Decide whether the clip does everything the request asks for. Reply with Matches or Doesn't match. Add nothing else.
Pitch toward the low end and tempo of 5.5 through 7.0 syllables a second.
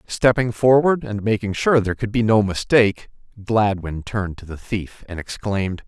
Doesn't match